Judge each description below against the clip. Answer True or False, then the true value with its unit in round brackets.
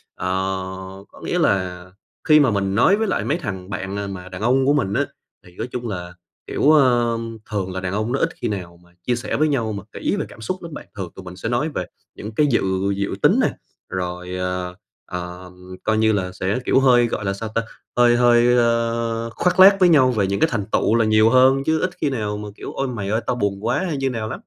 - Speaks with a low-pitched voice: True (110 Hz)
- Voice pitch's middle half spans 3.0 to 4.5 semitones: False (4.9 semitones)